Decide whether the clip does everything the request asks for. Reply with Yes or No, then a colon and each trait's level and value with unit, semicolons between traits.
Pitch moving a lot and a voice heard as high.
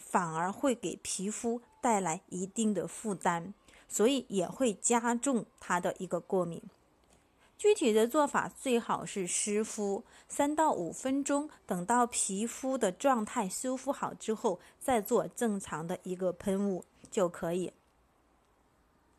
No: average, 5.0 semitones; high, 220 Hz